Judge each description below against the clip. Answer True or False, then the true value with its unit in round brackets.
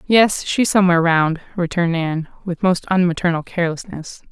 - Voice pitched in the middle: True (175 Hz)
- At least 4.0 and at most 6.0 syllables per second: True (5.5 syllables/s)